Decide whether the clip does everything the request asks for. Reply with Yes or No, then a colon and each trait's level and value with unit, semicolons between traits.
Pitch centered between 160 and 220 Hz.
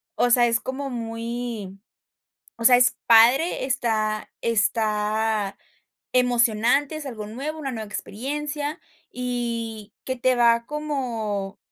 No: high, 235 Hz